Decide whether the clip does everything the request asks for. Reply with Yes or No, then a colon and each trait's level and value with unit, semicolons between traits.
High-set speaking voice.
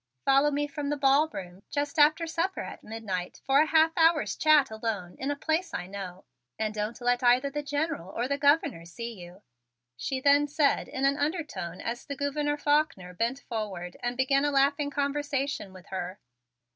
Yes: very high, 275 Hz